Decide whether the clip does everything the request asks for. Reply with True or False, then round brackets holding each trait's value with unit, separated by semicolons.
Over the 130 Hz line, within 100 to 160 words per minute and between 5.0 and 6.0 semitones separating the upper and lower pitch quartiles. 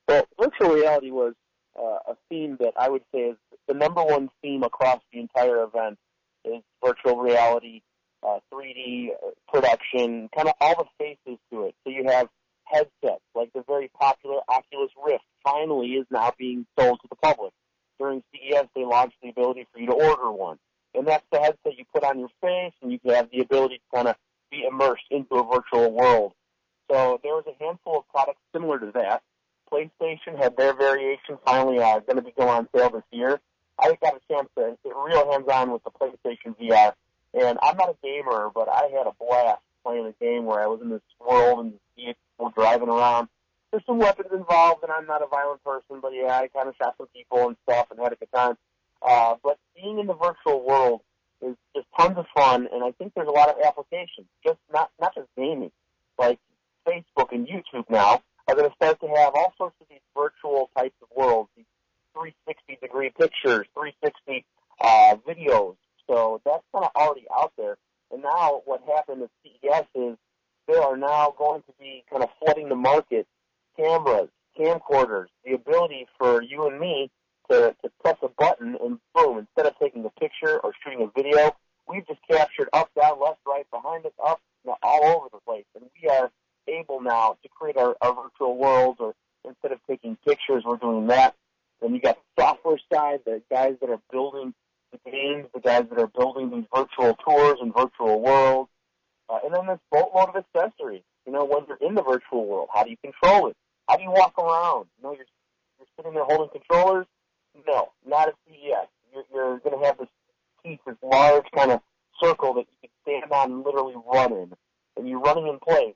False (140 Hz; 205 wpm; 5.4 semitones)